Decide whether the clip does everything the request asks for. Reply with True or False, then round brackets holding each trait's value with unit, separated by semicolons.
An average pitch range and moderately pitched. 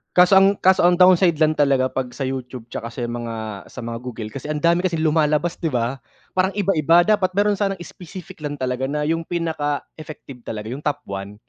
False (5.7 semitones; 150 Hz)